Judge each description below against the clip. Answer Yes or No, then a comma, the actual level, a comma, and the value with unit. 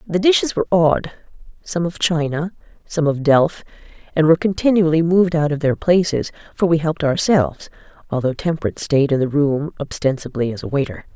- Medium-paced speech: Yes, average, 170 wpm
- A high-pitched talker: No, medium, 160 Hz